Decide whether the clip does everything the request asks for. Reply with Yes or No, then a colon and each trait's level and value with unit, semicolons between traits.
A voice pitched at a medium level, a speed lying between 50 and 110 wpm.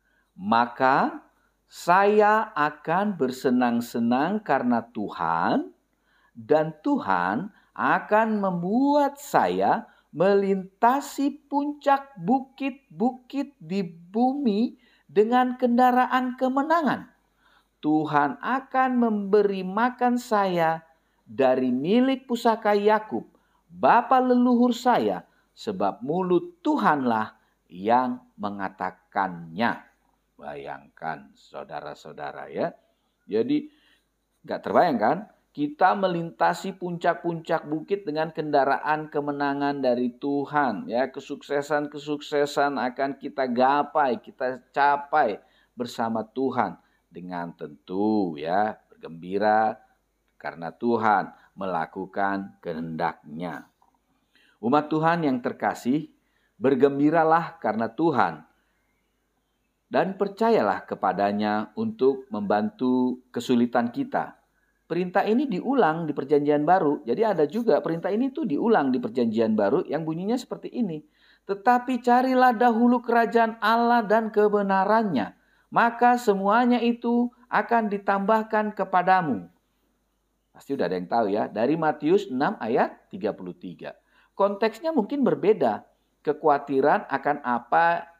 Yes: medium, 175 Hz; average, 90 wpm